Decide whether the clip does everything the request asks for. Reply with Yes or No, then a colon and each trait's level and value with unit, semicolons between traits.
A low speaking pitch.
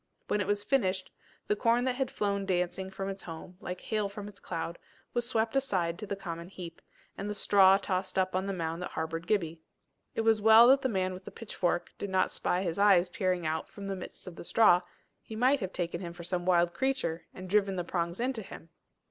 No: high, 190 Hz